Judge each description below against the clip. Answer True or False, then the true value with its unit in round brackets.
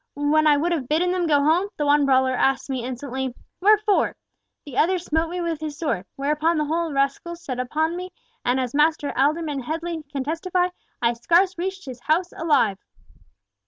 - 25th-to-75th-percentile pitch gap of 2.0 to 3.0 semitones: False (3.9 semitones)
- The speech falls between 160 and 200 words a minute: True (185 wpm)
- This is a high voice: True (305 Hz)